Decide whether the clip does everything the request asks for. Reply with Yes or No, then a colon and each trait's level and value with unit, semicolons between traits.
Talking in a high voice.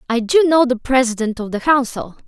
Yes: very high, 250 Hz